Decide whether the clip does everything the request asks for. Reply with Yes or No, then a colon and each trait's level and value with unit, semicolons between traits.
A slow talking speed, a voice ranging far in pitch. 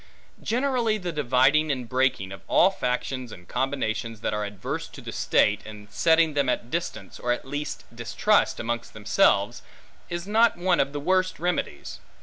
No: average, 165 wpm; wide, 7.1 semitones